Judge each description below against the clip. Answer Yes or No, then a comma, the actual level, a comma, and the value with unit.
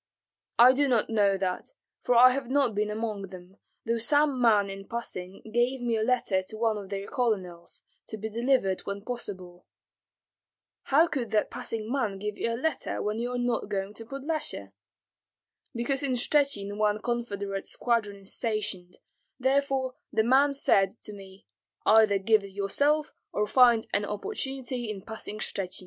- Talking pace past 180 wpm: No, average, 165 wpm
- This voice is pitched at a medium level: No, high, 220 Hz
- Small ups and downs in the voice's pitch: No, average, 4.0 semitones